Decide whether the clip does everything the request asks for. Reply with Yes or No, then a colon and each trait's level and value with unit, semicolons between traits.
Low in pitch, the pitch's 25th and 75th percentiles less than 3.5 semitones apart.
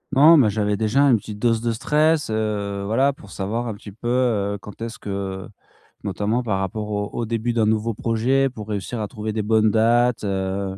Yes: low, 110 Hz; narrow, 2.5 semitones